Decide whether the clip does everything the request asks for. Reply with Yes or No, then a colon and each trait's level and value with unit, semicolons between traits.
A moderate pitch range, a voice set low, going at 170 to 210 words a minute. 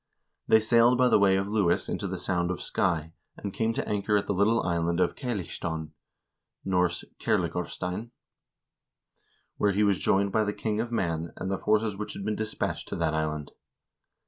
Yes: average, 3.7 semitones; low, 100 Hz; average, 180 wpm